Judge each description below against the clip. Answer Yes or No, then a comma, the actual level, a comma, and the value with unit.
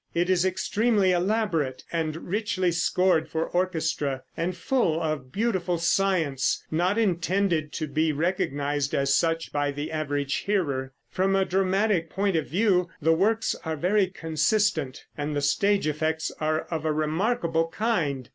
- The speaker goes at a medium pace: Yes, average, 145 wpm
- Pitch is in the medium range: Yes, medium, 165 Hz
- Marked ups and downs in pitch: No, average, 3.8 semitones